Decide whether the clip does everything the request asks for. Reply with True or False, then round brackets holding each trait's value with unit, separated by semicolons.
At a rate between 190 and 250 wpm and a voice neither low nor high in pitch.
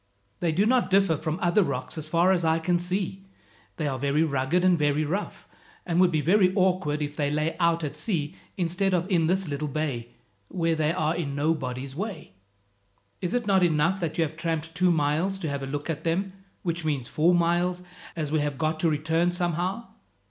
True (205 wpm; 165 Hz)